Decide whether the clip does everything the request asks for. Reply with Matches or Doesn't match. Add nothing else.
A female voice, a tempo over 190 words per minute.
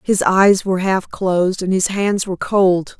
Matches